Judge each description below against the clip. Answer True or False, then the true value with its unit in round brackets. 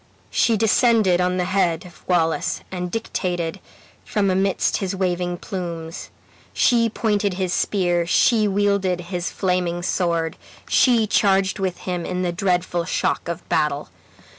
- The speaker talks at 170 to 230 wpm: False (140 wpm)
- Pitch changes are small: True (2.2 semitones)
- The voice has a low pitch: False (180 Hz)